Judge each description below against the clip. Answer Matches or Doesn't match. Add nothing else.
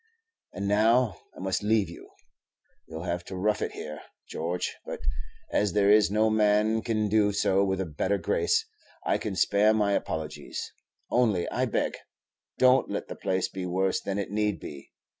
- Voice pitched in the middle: Doesn't match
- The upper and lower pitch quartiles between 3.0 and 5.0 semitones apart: Doesn't match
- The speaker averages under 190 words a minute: Matches